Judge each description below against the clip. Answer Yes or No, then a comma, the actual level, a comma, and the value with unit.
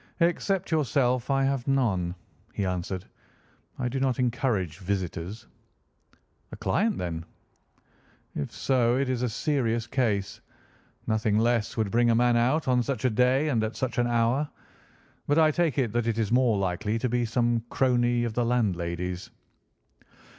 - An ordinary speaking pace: Yes, average, 160 wpm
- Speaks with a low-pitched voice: Yes, low, 120 Hz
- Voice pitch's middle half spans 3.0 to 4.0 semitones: Yes, average, 3.5 semitones